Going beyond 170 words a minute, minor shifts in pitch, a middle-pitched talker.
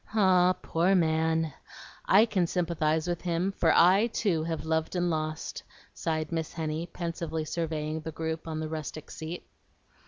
No: average, 155 wpm; narrow, 1.8 semitones; medium, 165 Hz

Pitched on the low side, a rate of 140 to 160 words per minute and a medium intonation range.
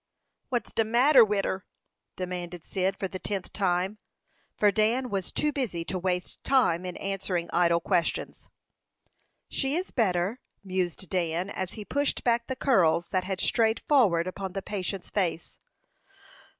No: high, 190 Hz; average, 150 wpm; average, 3.9 semitones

